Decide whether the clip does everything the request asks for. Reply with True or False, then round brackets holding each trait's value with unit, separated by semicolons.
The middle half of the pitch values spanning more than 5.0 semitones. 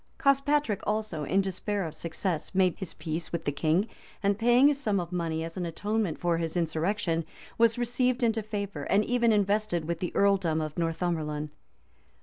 False (4.6 semitones)